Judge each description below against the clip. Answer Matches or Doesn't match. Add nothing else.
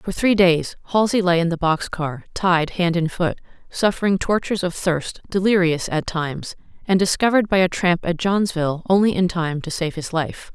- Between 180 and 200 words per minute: Matches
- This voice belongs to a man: Doesn't match